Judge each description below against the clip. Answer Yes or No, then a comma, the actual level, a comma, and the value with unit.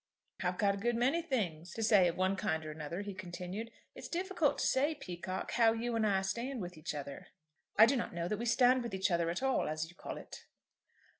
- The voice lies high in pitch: Yes, high, 200 Hz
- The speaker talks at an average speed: No, fast, 230 wpm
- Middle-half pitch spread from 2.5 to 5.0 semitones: No, wide, 5.4 semitones